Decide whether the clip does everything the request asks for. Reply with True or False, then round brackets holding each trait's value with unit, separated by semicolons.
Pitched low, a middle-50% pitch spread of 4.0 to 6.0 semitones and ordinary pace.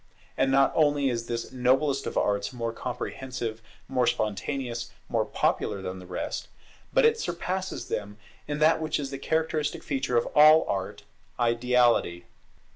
True (125 Hz; 4.3 semitones; 150 wpm)